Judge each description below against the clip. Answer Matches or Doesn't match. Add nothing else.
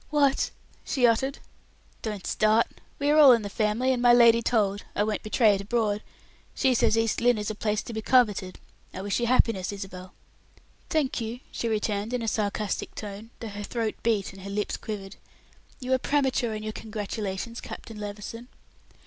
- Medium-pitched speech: Doesn't match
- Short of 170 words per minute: Doesn't match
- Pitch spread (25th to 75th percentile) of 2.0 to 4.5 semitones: Matches